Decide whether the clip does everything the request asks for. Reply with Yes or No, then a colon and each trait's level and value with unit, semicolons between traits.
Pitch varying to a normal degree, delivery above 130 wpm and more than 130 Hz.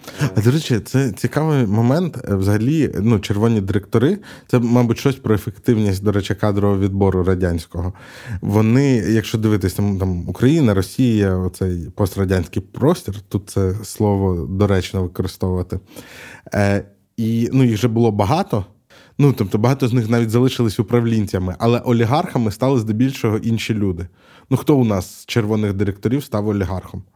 No: average, 3.8 semitones; average, 140 wpm; low, 110 Hz